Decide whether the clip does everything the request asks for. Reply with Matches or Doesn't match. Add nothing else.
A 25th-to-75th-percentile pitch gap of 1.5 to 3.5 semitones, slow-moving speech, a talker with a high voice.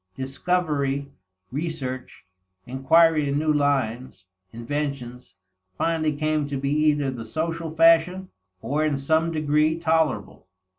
Doesn't match